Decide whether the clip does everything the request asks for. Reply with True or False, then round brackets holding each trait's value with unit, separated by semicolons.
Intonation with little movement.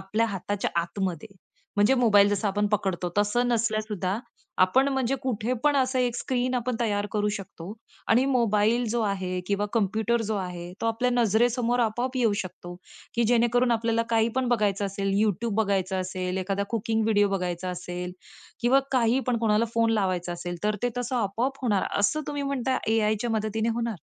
False (3.4 semitones)